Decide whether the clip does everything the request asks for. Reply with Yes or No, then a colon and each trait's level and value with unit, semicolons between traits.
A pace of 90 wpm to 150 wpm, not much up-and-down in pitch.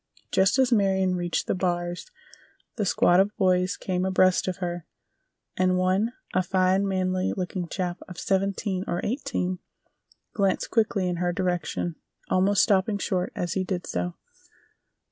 Yes: average, 140 wpm; narrow, 1.4 semitones